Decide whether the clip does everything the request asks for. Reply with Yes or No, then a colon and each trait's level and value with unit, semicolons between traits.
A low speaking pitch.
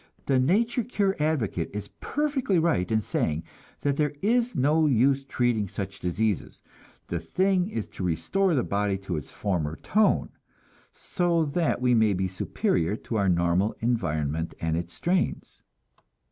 Yes: low, 115 Hz